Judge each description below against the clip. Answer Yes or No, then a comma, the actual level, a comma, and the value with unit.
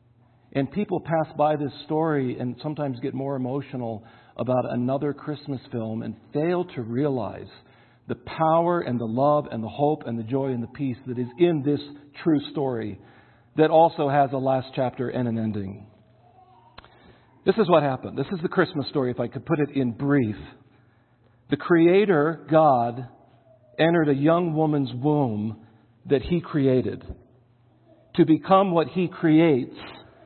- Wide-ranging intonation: No, average, 4.2 semitones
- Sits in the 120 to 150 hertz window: Yes, low, 135 Hz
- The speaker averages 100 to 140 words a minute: No, average, 160 wpm